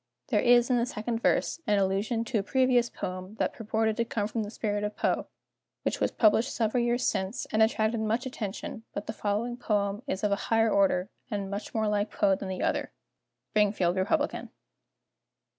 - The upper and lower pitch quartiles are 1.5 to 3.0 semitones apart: Yes, narrow, 2.6 semitones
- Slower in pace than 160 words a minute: No, average, 190 wpm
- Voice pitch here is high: Yes, high, 215 Hz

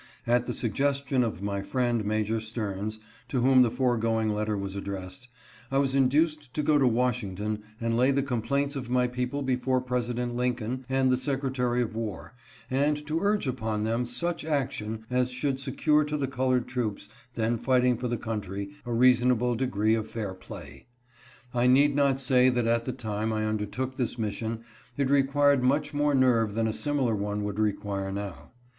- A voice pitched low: Yes, low, 125 Hz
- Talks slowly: No, average, 180 wpm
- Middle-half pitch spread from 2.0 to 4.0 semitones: Yes, average, 3.4 semitones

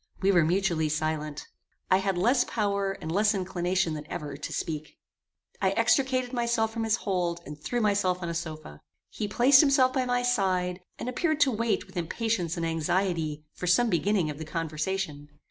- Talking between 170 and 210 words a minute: Yes, average, 180 wpm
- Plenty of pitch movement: Yes, wide, 5.8 semitones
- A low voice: No, medium, 185 Hz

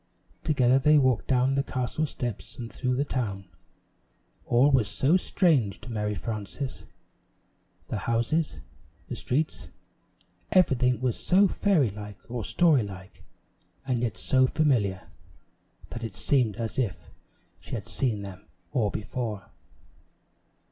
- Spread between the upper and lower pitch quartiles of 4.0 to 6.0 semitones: Yes, average, 4.5 semitones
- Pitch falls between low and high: No, low, 125 Hz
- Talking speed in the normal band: No, slow, 130 wpm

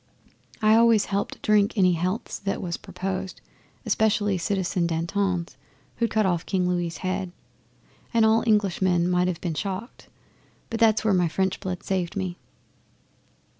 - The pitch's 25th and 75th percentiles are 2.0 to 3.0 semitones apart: Yes, average, 2.7 semitones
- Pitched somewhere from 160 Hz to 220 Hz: Yes, high, 190 Hz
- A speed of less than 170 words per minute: Yes, average, 145 wpm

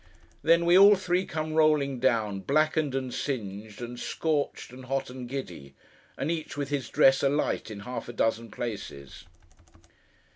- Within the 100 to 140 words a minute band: No, average, 155 wpm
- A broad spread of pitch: No, average, 5.0 semitones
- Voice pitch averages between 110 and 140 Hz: Yes, low, 135 Hz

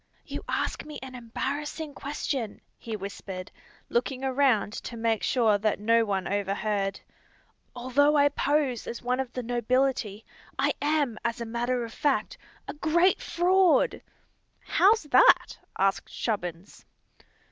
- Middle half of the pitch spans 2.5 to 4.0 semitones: No, average, 5.0 semitones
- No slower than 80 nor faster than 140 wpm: Yes, slow, 135 wpm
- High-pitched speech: Yes, high, 245 Hz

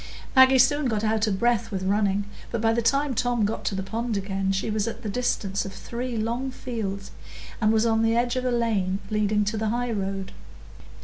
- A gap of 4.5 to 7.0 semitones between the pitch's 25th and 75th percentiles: No, average, 3.2 semitones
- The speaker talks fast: Yes, fast, 210 wpm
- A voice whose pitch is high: Yes, high, 220 Hz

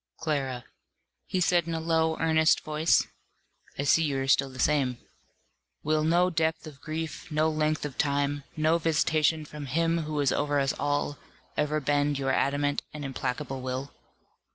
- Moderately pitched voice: Yes, medium, 150 Hz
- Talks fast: No, average, 165 wpm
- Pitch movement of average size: No, narrow, 2.2 semitones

